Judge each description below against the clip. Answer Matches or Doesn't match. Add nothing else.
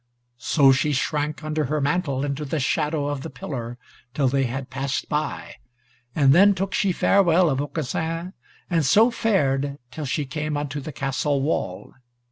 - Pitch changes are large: Doesn't match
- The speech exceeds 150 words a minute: Matches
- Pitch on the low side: Doesn't match